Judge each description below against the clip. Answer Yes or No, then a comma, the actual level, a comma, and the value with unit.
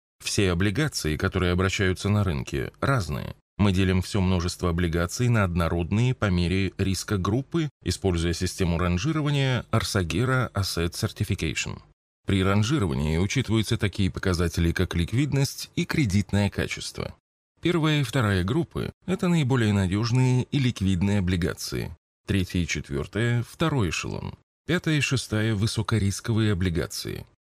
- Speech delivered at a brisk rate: No, average, 120 wpm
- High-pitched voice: No, low, 100 Hz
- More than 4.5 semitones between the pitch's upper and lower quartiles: Yes, average, 5.1 semitones